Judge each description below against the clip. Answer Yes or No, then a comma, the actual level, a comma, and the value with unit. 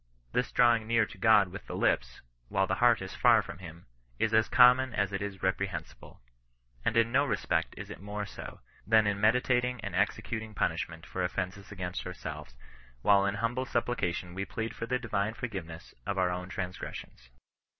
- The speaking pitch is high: No, low, 105 Hz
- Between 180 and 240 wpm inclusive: Yes, average, 185 wpm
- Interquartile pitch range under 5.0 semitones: Yes, average, 3.7 semitones